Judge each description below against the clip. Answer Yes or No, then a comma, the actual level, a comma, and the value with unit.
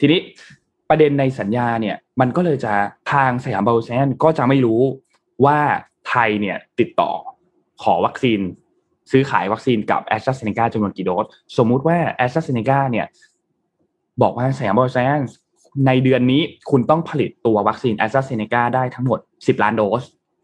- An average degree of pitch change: Yes, average, 3.3 semitones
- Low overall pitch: Yes, low, 130 Hz